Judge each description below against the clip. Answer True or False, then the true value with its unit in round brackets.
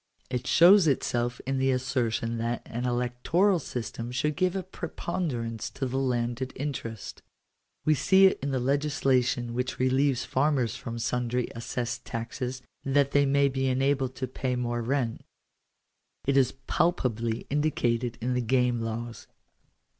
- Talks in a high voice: False (125 Hz)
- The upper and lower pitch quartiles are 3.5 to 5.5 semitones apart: False (2.7 semitones)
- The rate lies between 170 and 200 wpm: False (145 wpm)